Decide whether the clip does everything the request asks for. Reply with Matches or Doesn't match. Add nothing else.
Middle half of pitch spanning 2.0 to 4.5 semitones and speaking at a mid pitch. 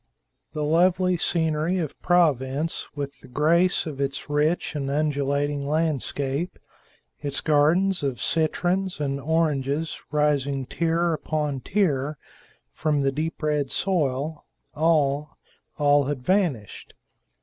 Matches